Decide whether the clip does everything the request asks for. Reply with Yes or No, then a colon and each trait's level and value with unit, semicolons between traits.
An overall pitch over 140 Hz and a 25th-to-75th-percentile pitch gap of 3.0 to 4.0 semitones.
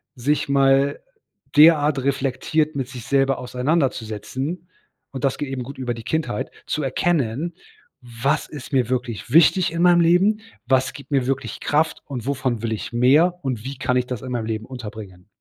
No: low, 135 Hz; average, 3.3 semitones